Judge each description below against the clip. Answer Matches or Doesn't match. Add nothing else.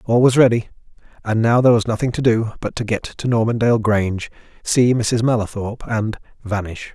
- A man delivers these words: Matches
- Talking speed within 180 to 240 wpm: Doesn't match